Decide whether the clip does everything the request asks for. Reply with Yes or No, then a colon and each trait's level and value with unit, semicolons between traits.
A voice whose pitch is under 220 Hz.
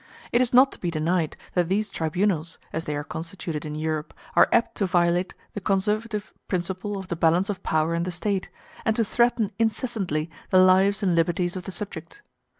Yes: medium, 185 Hz